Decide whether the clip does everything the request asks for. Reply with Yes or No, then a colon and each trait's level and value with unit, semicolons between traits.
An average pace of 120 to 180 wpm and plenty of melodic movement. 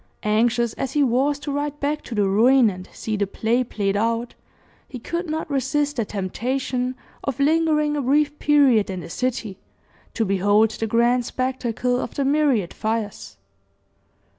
No: average, 165 wpm; average, 4.7 semitones